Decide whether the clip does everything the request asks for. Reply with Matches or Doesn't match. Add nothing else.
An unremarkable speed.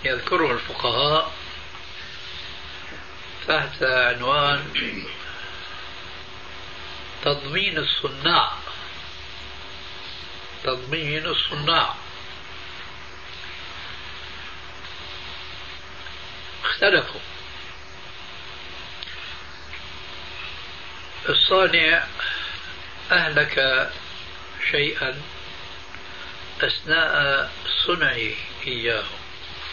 Doesn't match